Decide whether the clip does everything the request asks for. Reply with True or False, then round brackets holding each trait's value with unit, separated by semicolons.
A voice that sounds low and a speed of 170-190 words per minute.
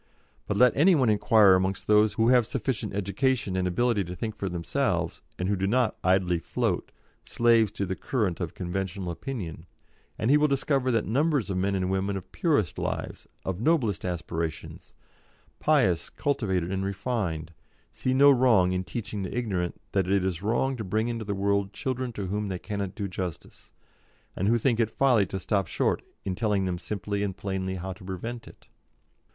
True (100 Hz; 185 wpm)